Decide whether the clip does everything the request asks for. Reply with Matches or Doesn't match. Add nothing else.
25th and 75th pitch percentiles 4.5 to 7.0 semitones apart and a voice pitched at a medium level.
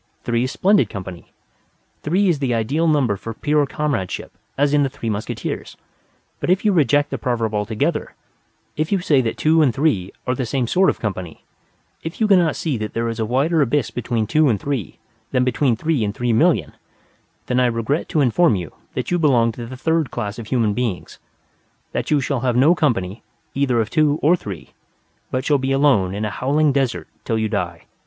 Doesn't match